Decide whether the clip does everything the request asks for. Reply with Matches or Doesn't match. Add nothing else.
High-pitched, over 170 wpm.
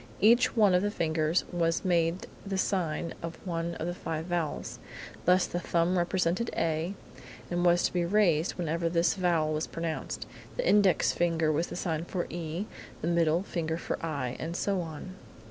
Doesn't match